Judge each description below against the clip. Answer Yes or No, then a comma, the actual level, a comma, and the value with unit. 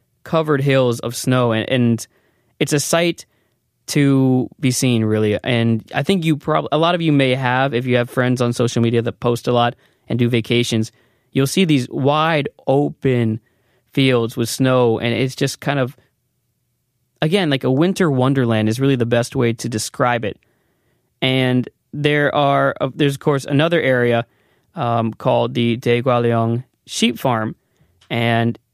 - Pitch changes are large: No, average, 2.7 semitones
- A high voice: No, low, 125 Hz